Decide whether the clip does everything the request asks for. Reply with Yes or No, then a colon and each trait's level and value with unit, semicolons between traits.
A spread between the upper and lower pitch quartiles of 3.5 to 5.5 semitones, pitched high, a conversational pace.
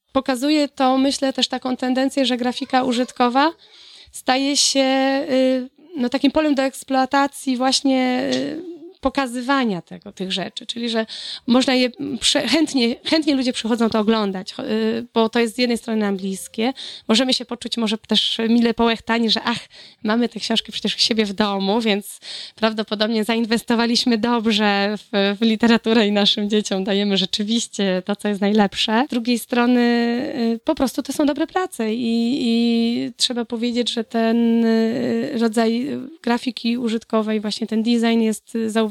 No: average, 2.8 semitones; high, 235 Hz; average, 145 wpm